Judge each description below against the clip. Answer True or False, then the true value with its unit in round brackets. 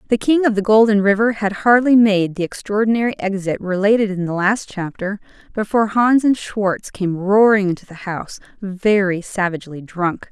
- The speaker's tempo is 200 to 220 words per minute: False (170 wpm)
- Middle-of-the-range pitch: False (205 Hz)